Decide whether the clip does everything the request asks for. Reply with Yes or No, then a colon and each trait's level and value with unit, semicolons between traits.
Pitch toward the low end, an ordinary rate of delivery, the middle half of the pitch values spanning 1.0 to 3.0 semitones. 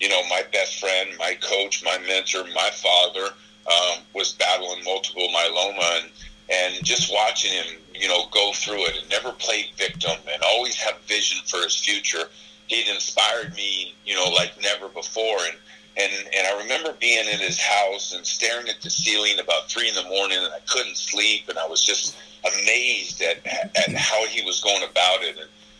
Yes: low, 100 Hz; average, 190 wpm; average, 2.7 semitones